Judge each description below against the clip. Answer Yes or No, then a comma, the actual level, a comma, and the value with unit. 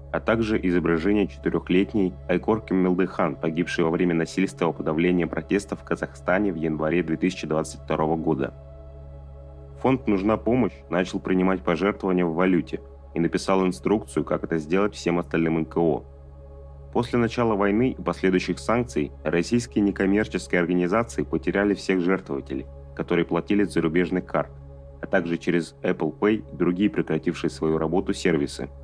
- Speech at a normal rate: Yes, average, 130 wpm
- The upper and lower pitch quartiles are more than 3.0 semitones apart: Yes, average, 3.7 semitones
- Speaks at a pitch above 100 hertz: No, very low, 85 Hz